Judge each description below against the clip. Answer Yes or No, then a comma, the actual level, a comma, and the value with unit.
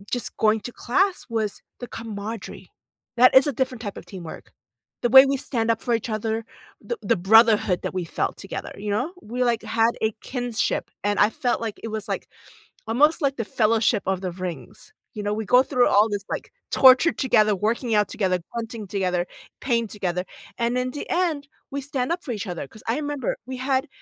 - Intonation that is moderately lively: Yes, average, 3.6 semitones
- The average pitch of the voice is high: Yes, high, 230 Hz